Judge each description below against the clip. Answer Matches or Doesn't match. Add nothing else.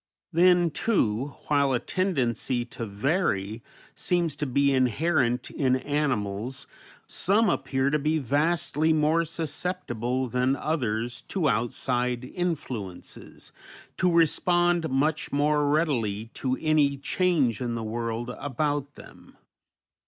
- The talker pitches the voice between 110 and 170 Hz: Matches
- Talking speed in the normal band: Doesn't match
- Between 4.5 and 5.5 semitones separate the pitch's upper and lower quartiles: Matches